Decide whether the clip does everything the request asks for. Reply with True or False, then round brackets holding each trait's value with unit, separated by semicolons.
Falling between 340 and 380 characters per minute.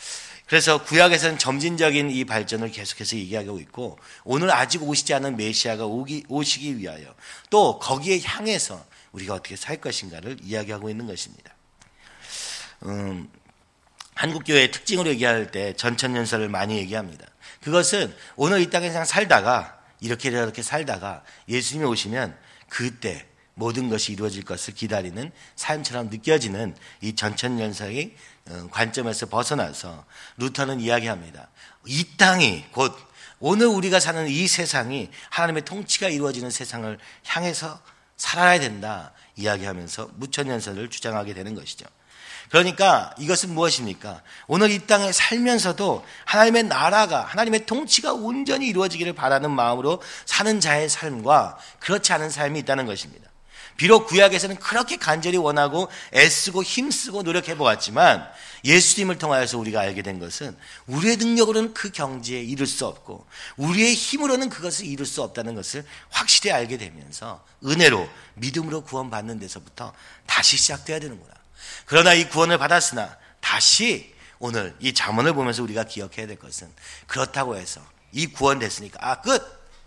True (350 characters per minute)